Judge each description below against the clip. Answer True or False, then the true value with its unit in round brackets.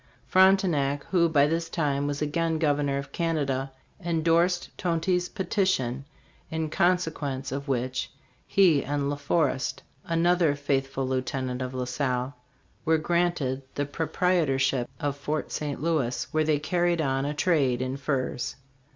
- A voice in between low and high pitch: True (145 Hz)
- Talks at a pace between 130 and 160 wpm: True (140 wpm)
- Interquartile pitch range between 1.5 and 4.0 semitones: True (3.7 semitones)